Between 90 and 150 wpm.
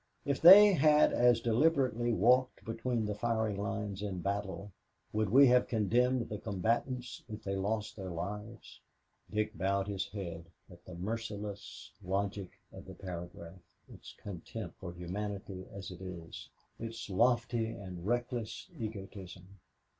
Yes: average, 140 wpm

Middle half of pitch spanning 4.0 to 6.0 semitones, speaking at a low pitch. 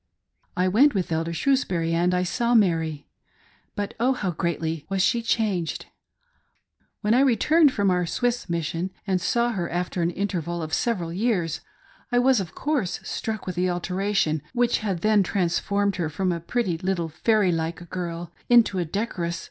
No: average, 4.6 semitones; medium, 185 Hz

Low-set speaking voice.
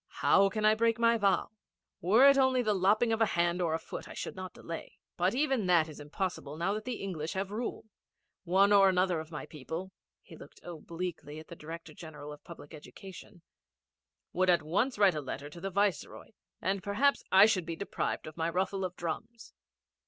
No: medium, 185 Hz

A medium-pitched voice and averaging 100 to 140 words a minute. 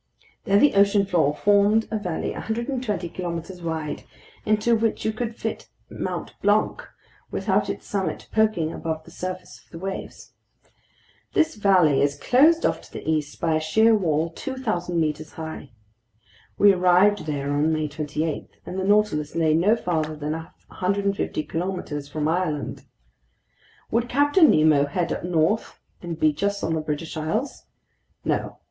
No: medium, 175 Hz; average, 155 wpm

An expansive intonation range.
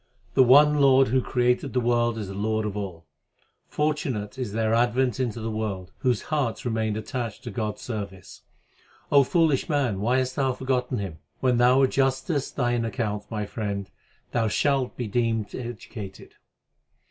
No: average, 3.6 semitones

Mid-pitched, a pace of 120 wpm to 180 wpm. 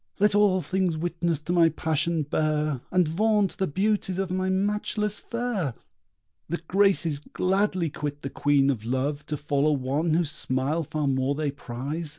Yes: medium, 160 Hz; average, 160 wpm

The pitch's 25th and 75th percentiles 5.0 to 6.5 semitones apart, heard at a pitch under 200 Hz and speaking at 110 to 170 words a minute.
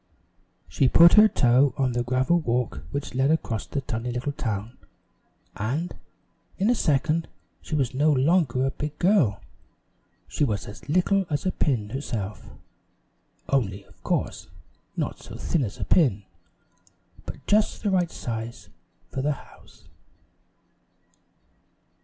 Yes: average, 5.3 semitones; low, 135 Hz; average, 140 wpm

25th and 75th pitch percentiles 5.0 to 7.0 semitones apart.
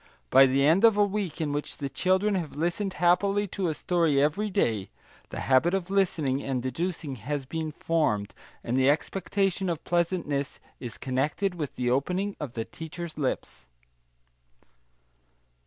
Yes: wide, 5.4 semitones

